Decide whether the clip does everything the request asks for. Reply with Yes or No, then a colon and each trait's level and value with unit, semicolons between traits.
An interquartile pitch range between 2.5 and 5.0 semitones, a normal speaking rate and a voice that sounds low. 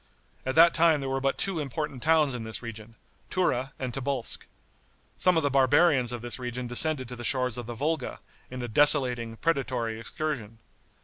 Yes: average, 3.7 semitones; average, 185 wpm; low, 130 Hz